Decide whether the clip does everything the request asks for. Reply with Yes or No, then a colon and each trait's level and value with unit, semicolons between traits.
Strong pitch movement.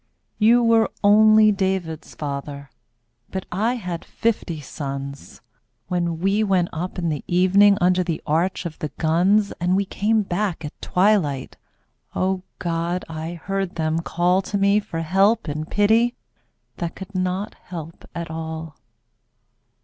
No: average, 3.7 semitones